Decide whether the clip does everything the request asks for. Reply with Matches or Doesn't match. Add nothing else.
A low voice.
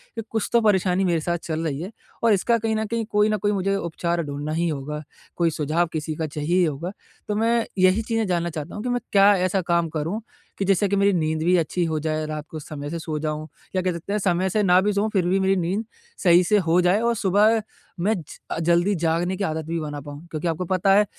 Doesn't match